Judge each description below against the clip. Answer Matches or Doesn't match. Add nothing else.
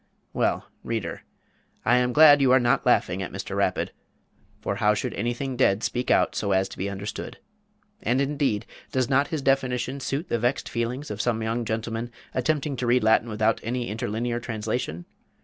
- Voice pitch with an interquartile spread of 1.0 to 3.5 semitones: Matches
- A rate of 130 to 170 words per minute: Doesn't match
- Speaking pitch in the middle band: Doesn't match